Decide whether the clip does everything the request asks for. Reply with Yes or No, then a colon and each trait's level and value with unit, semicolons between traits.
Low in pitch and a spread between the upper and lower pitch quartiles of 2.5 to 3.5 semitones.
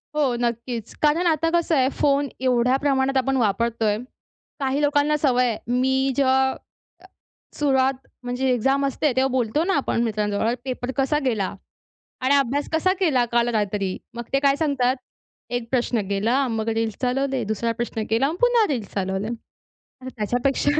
No: very high, 260 Hz; average, 3.0 semitones